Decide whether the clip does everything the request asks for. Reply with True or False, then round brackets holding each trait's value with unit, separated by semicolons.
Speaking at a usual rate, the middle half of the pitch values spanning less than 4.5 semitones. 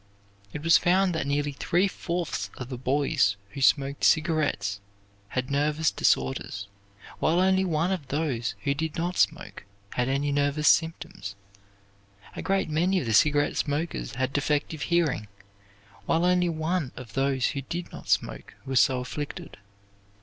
True (150 wpm; 4.1 semitones)